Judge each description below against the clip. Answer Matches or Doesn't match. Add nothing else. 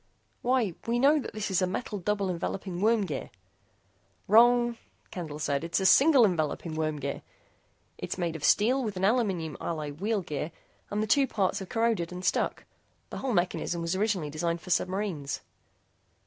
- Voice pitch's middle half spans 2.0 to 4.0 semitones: Doesn't match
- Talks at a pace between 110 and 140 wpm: Doesn't match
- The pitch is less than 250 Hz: Matches